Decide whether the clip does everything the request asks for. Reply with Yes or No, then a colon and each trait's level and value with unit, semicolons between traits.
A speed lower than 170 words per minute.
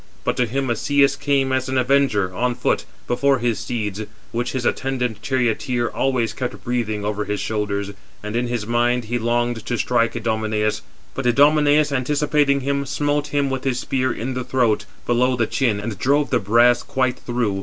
No: average, 185 wpm